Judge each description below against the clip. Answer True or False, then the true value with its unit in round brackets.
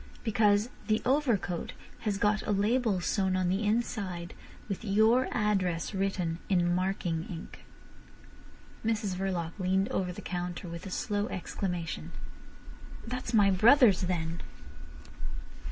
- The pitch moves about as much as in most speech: True (3.2 semitones)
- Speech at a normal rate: False (120 wpm)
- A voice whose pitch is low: False (195 Hz)